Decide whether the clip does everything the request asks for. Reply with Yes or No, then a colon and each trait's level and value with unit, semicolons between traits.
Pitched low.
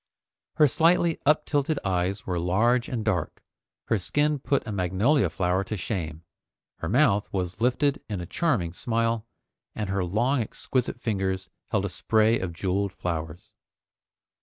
Yes: low, 105 Hz